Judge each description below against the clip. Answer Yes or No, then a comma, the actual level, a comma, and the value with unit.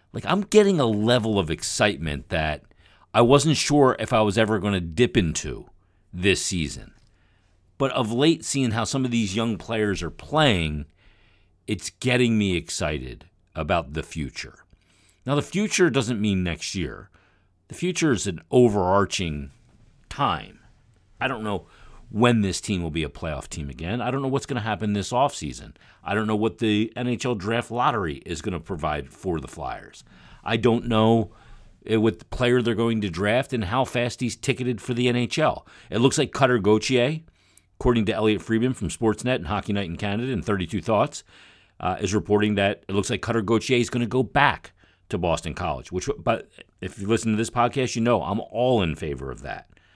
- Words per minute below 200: Yes, average, 190 wpm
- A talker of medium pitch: No, low, 110 Hz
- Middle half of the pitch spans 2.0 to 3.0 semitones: No, average, 4.7 semitones